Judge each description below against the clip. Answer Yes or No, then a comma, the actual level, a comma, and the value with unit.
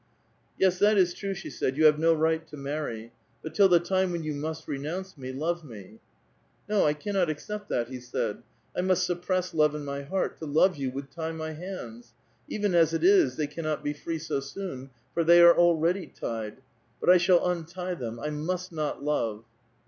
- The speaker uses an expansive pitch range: No, average, 4.0 semitones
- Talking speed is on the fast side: Yes, fast, 210 wpm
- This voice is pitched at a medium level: Yes, medium, 160 Hz